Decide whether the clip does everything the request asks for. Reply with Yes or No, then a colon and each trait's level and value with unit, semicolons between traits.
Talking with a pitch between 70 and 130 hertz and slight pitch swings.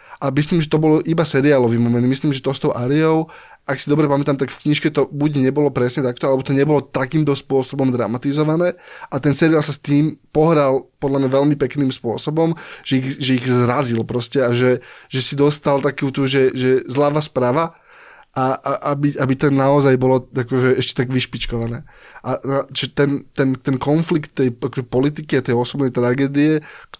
No: medium, 140 Hz; narrow, 2.3 semitones